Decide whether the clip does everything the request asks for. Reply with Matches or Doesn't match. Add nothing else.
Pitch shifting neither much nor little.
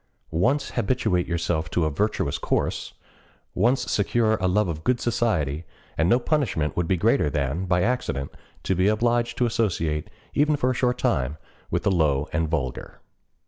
Doesn't match